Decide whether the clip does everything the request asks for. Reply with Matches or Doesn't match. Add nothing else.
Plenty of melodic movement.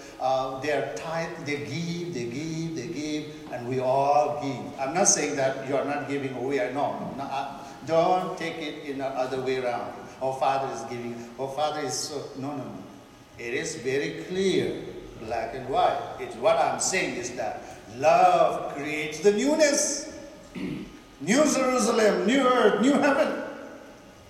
Matches